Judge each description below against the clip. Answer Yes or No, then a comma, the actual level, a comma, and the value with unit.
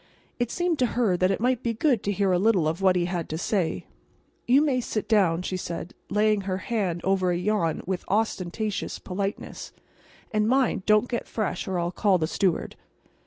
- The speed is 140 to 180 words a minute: No, average, 190 wpm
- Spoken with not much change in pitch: No, average, 3.7 semitones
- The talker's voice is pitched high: Yes, high, 195 Hz